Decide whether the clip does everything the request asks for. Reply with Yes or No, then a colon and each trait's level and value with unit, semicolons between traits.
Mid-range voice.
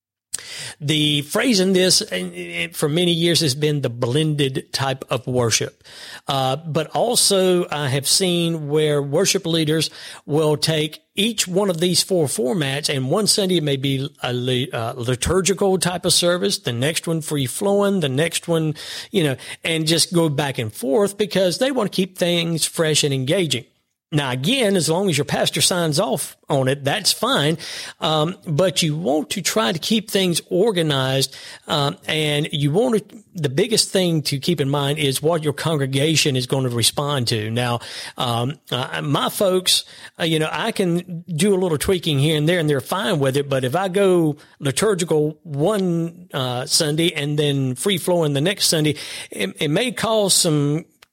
Yes: medium, 160 Hz